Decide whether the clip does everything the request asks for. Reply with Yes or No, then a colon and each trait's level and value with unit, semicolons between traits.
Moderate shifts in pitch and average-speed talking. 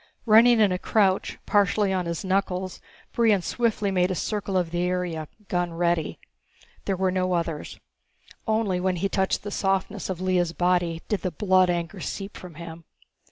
No: narrow, 2.0 semitones; average, 170 wpm